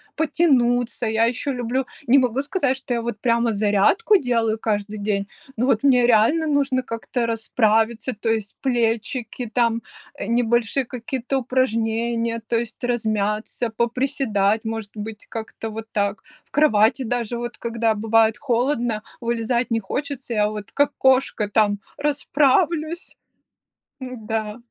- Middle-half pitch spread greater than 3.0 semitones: No, average, 2.7 semitones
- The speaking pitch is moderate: No, high, 235 Hz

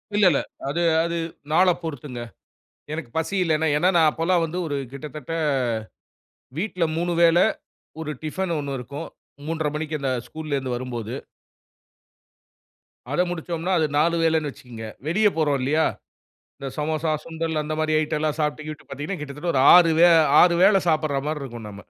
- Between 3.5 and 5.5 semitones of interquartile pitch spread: No, narrow, 2.5 semitones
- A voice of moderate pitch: Yes, medium, 155 Hz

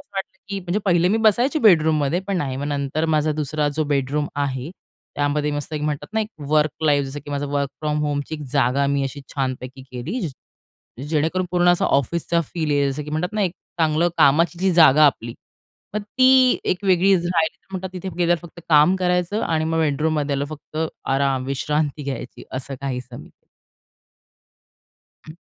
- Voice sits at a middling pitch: Yes, medium, 150 Hz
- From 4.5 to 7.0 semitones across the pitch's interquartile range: No, average, 3.8 semitones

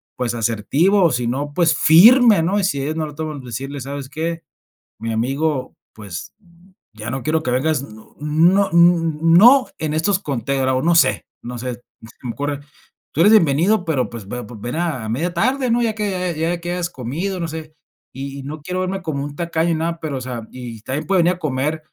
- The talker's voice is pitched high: No, medium, 155 Hz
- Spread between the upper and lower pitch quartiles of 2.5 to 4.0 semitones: No, average, 4.8 semitones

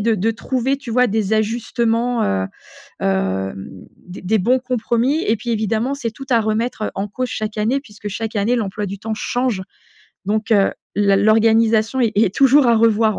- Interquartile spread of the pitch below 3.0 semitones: Yes, narrow, 2.5 semitones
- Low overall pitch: No, high, 220 Hz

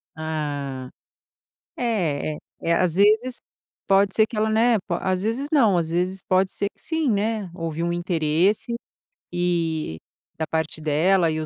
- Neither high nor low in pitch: Yes, medium, 180 Hz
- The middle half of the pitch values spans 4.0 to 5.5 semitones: Yes, average, 5.0 semitones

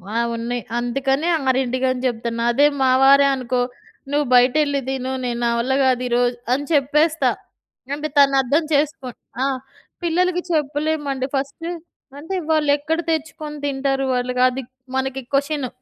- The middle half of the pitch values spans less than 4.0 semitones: Yes, average, 2.8 semitones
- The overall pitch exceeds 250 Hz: Yes, very high, 275 Hz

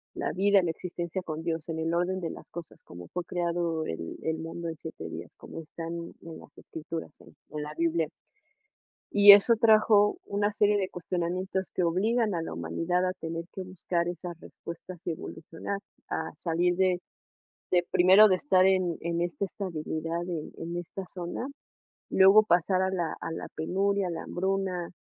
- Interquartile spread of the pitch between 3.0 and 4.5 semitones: No, narrow, 2.4 semitones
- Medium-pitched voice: Yes, medium, 175 Hz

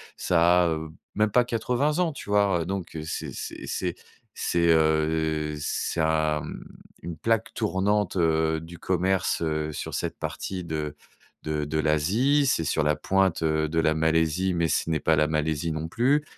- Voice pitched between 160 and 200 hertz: No, very low, 80 Hz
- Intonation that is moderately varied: Yes, average, 3.6 semitones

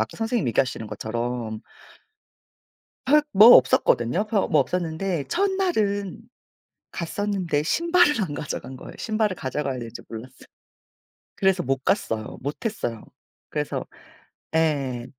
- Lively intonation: Yes, wide, 8.6 semitones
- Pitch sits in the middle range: Yes, medium, 160 Hz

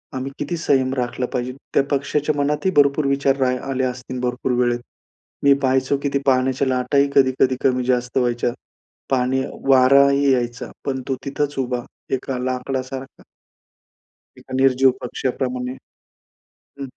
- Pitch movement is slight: Yes, narrow, 1.6 semitones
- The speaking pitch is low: Yes, low, 130 Hz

